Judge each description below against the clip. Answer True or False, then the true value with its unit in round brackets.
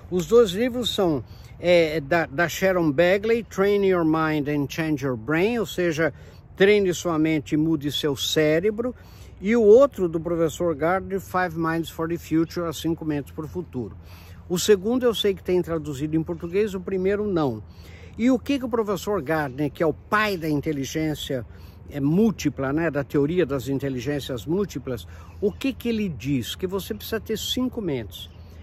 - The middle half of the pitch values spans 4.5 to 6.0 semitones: True (5.3 semitones)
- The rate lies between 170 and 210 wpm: True (180 wpm)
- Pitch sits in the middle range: True (165 Hz)